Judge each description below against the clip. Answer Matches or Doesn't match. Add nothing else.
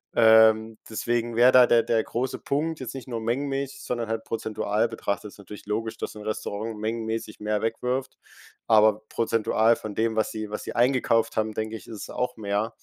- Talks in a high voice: Doesn't match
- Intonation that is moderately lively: Doesn't match